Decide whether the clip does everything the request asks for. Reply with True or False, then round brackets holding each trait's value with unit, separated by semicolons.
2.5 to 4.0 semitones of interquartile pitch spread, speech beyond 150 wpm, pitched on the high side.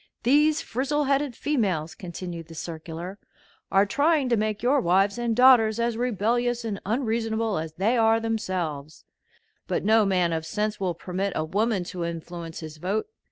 False (5.5 semitones; 160 wpm; 210 Hz)